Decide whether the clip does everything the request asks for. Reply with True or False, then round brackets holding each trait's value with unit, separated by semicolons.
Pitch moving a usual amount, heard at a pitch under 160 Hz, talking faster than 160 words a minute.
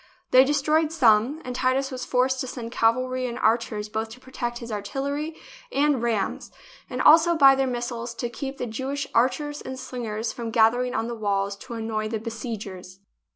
False (3.1 semitones; 245 Hz; 185 wpm)